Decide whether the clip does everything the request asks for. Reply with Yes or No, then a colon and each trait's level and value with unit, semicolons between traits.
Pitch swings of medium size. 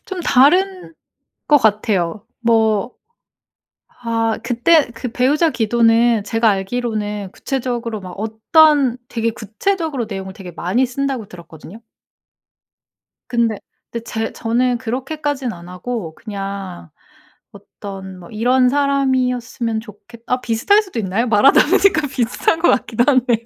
Yes: average, 3.7 semitones